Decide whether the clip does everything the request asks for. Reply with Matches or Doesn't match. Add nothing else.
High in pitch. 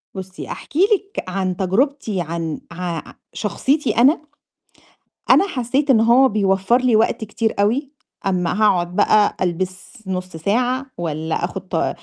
Matches